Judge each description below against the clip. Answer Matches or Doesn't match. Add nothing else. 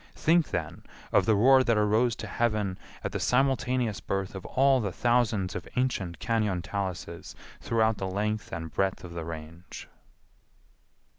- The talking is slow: Doesn't match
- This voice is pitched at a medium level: Doesn't match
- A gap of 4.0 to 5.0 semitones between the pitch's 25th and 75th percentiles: Matches